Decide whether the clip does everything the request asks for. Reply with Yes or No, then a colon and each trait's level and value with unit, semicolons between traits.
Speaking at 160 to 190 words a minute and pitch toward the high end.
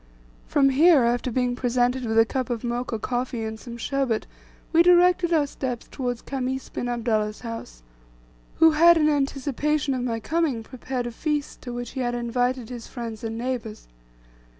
Yes: average, 175 wpm; very high, 250 Hz